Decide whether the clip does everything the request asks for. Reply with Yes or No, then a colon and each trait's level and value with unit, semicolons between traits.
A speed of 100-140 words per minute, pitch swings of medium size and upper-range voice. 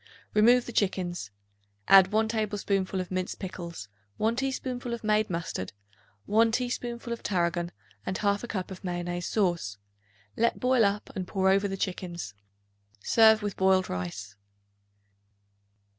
Yes: slow, 135 wpm; average, 3.9 semitones; high, 195 Hz